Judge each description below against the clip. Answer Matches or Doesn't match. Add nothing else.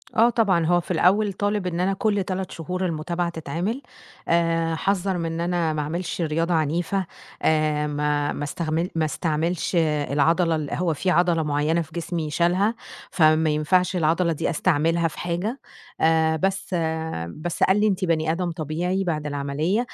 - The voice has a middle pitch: Matches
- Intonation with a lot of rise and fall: Doesn't match